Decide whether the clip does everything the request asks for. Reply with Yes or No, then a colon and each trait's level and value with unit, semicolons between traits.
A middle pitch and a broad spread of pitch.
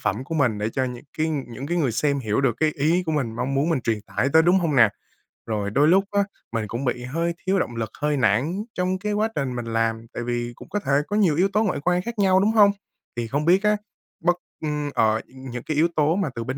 Yes: medium, 145 Hz; wide, 6.6 semitones